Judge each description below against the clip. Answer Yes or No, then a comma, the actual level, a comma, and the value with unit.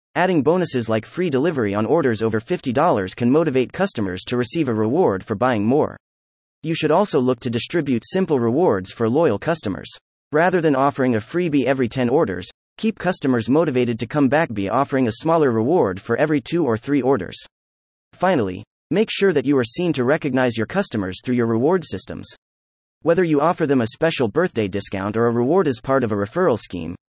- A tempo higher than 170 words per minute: Yes, average, 190 wpm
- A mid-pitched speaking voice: No, low, 130 Hz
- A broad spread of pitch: Yes, wide, 6.6 semitones